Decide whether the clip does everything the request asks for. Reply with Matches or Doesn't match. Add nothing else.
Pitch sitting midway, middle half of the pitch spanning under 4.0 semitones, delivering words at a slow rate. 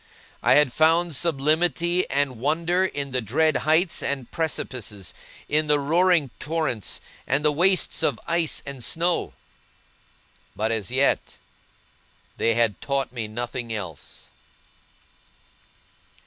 Doesn't match